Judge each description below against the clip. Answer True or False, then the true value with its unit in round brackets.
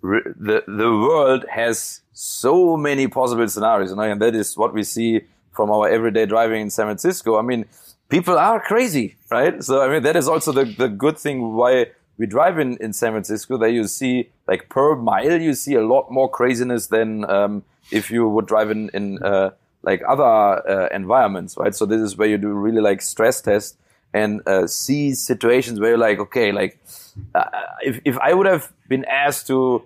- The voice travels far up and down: False (3.3 semitones)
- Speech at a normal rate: False (200 wpm)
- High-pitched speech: False (115 Hz)